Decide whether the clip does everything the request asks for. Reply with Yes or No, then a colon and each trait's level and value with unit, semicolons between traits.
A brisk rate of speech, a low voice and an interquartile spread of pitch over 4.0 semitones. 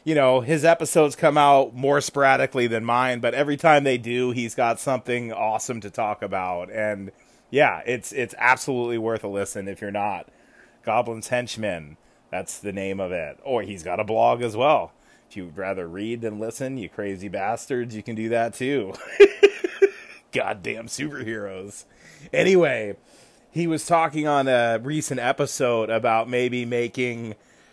No: average, 160 wpm; low, 120 Hz; average, 4.4 semitones